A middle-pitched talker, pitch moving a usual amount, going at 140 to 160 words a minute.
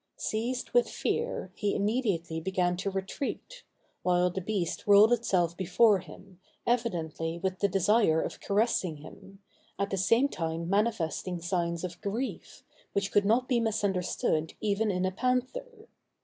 No: high, 195 Hz; average, 4.4 semitones; average, 145 wpm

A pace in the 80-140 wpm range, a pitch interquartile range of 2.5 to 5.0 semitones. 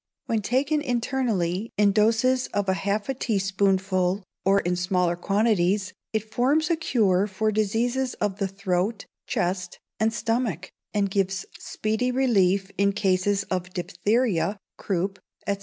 Yes: slow, 135 wpm; average, 3.2 semitones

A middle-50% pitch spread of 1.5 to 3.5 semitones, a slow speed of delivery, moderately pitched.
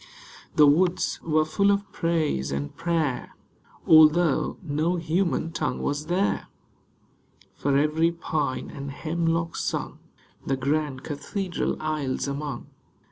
Yes: average, 2.8 semitones; slow, 115 wpm; medium, 155 Hz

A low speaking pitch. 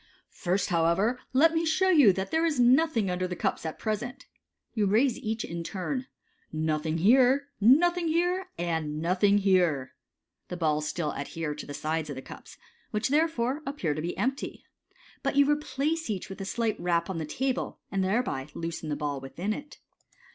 No: high, 200 Hz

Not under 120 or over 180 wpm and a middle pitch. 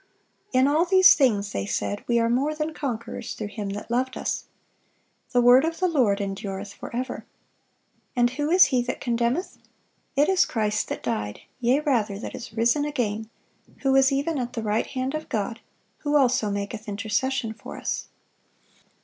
No: average, 175 wpm; high, 245 Hz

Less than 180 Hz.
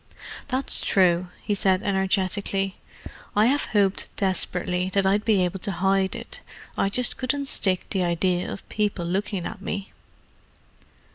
No: high, 195 Hz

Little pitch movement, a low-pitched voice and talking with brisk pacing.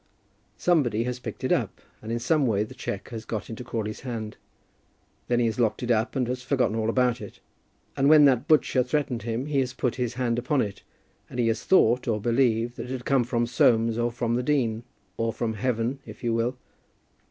Yes: narrow, 2.1 semitones; low, 120 Hz; fast, 220 wpm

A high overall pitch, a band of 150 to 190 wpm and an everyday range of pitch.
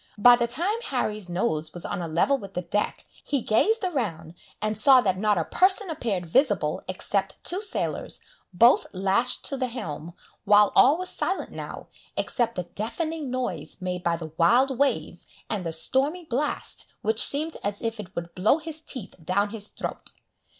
No: high, 220 Hz; average, 180 wpm; wide, 7.3 semitones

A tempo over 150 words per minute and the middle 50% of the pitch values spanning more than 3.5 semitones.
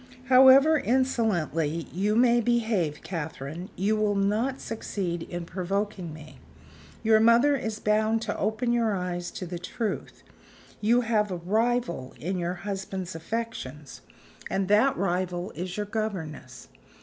No: slow, 135 wpm; average, 4.4 semitones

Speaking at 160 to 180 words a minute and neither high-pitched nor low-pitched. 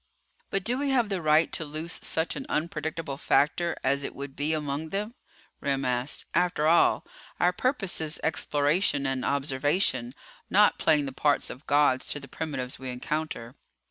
Yes: average, 170 wpm; medium, 150 Hz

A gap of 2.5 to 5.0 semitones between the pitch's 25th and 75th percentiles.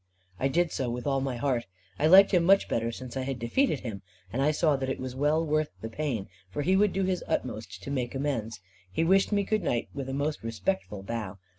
No: wide, 5.6 semitones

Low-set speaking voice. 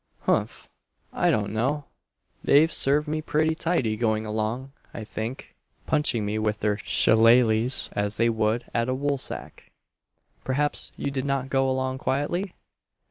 Yes: low, 130 Hz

